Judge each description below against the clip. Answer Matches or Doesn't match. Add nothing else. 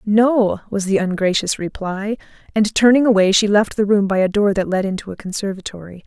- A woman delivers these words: Matches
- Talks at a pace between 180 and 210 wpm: Matches